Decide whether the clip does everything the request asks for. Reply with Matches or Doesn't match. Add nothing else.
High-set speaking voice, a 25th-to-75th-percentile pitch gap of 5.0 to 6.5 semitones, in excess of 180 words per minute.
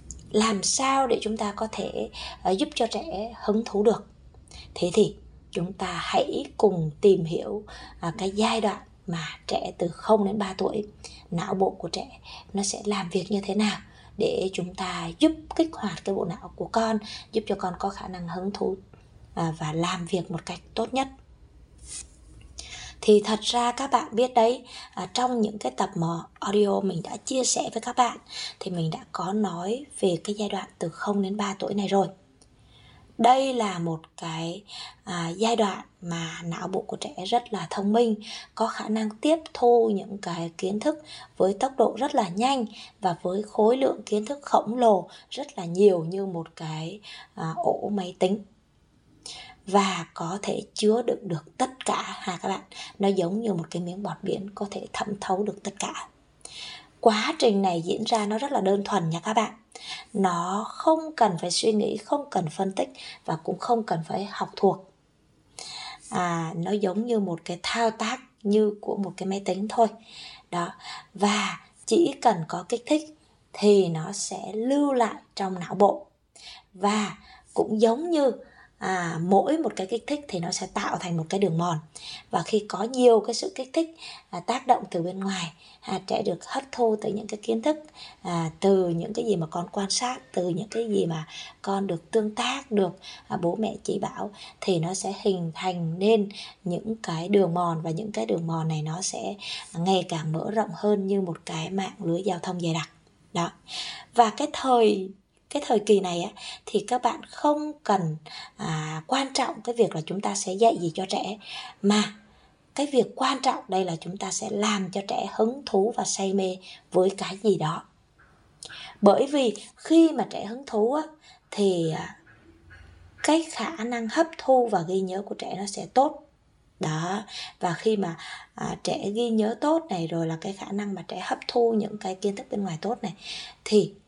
Doesn't match